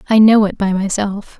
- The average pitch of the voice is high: Yes, high, 205 Hz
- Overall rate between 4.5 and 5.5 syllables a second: Yes, 5.0 syllables/s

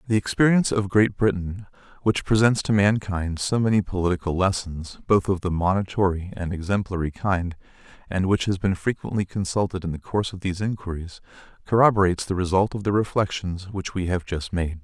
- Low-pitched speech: Yes, very low, 95 Hz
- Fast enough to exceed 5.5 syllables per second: Yes, 5.7 syllables/s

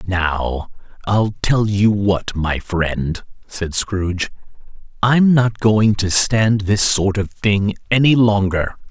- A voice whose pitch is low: Yes, low, 100 Hz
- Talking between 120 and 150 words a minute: Yes, average, 140 wpm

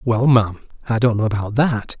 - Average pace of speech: No, fast, 210 wpm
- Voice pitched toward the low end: Yes, low, 115 Hz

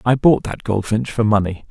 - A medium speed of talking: No, fast, 210 wpm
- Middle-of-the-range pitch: No, low, 110 Hz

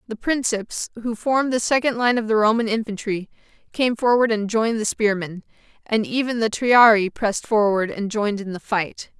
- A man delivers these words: No, female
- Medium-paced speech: Yes, average, 185 wpm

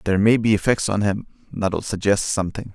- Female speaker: No, male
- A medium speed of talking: Yes, average, 195 wpm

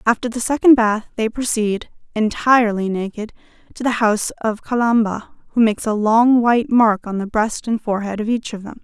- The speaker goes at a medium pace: Yes, average, 190 wpm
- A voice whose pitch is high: Yes, high, 225 Hz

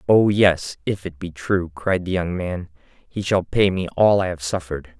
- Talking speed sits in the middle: No, fast, 215 wpm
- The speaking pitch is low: Yes, very low, 90 Hz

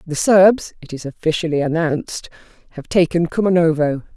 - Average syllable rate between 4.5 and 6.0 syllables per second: Yes, 5.3 syllables/s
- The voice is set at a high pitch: No, medium, 165 Hz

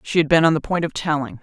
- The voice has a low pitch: No, medium, 155 Hz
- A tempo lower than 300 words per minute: No, fast, 335 wpm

